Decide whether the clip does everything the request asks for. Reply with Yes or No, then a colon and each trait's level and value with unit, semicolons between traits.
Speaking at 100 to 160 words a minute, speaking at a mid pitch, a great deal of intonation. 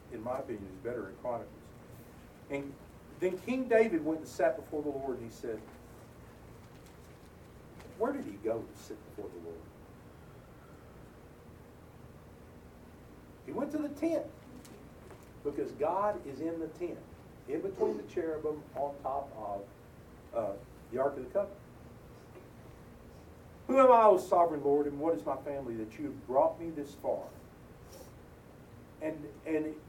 Yes: average, 145 wpm; medium, 150 Hz; wide, 8.8 semitones